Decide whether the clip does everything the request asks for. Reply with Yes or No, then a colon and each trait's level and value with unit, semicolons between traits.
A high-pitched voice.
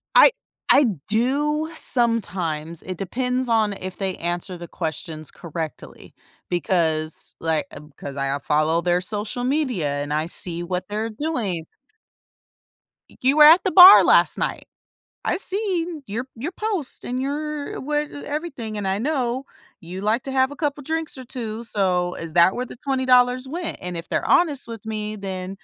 Yes: high, 225 Hz